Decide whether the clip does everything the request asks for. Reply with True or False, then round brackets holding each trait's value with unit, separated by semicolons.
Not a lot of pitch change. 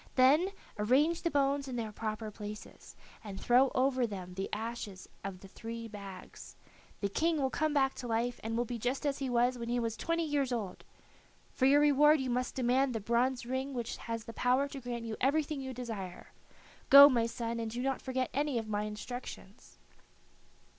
False (3.3 semitones)